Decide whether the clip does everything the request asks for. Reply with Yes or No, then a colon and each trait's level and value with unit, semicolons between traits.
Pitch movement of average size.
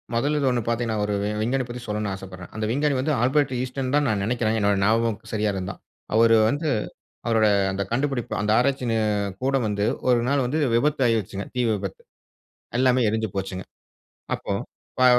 Yes: average, 3.8 semitones